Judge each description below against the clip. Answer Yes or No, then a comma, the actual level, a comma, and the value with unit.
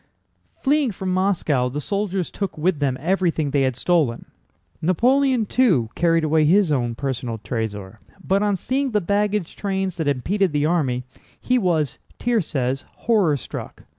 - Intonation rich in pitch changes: Yes, wide, 6.7 semitones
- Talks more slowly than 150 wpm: No, average, 155 wpm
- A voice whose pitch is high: No, medium, 170 Hz